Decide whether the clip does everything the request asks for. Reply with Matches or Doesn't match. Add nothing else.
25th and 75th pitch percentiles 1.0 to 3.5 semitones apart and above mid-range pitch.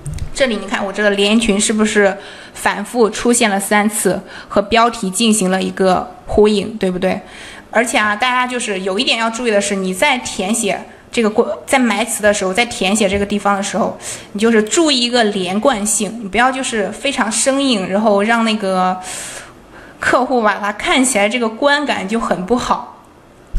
Matches